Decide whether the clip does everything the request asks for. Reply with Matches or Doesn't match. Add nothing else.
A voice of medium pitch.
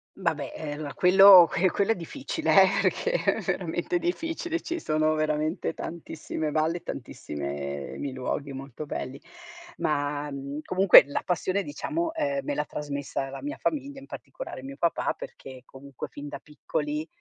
Matches